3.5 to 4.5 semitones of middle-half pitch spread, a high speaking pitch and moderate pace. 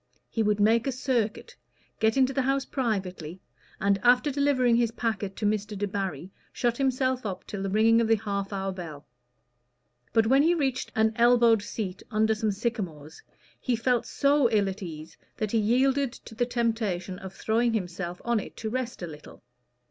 Yes: average, 3.8 semitones; high, 220 Hz; average, 180 wpm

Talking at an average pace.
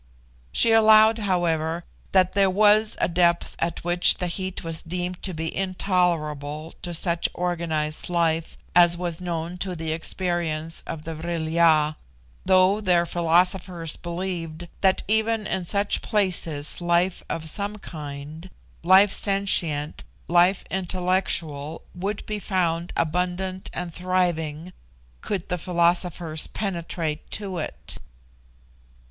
No: slow, 125 wpm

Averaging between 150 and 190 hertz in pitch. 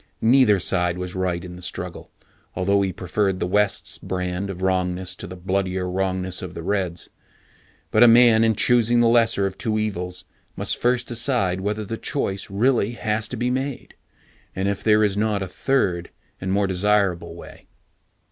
No: low, 100 Hz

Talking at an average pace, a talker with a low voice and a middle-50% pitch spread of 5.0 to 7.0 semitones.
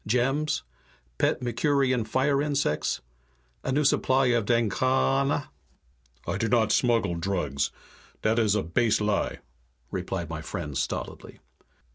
No: slow, 120 wpm; low, 115 Hz; average, 5.3 semitones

